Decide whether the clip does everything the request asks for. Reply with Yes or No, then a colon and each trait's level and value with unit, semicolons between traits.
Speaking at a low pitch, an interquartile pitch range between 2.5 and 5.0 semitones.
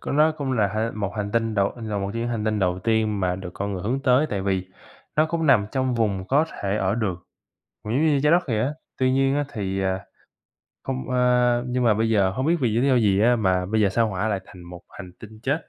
Yes: low, 110 Hz; average, 4.6 semitones